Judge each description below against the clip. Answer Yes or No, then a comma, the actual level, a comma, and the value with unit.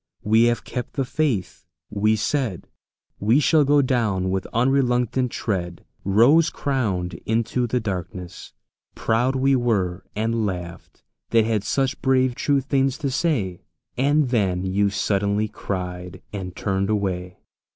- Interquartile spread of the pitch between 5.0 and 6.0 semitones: Yes, average, 5.3 semitones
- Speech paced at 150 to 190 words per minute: No, slow, 135 wpm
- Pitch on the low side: Yes, low, 110 Hz